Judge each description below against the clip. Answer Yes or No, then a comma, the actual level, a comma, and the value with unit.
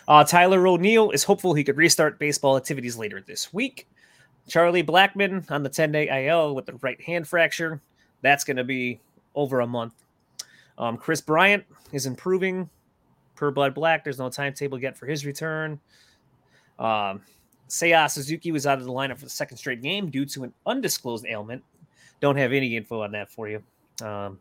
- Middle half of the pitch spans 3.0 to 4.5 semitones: Yes, average, 4.2 semitones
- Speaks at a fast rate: No, average, 180 wpm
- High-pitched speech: No, medium, 140 Hz